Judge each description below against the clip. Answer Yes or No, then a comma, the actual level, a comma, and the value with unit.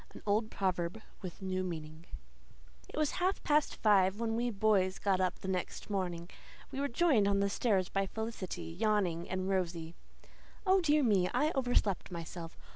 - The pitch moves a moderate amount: Yes, average, 3.8 semitones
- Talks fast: No, average, 175 wpm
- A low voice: No, high, 195 Hz